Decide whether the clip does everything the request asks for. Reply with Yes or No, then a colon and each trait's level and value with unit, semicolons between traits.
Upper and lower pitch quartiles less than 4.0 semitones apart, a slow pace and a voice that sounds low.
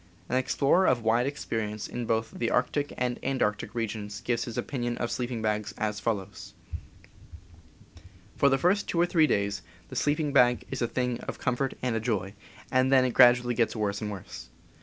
No: average, 3.3 semitones; average, 185 wpm; low, 120 Hz